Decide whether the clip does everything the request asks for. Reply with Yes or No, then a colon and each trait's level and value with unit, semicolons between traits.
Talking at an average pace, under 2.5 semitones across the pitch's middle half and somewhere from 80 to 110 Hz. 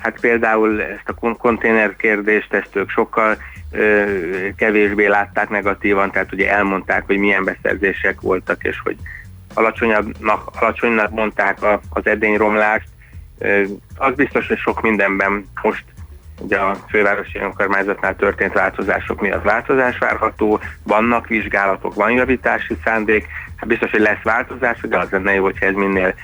Yes: average, 140 wpm; narrow, 2.0 semitones; low, 105 Hz